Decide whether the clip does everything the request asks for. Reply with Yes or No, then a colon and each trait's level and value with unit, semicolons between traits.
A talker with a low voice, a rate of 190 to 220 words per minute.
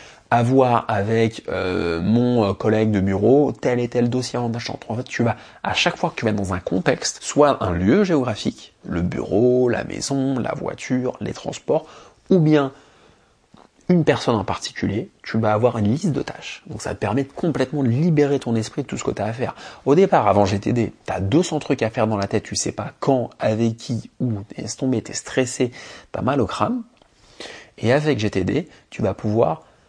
Yes: low, 120 Hz; fast, 205 wpm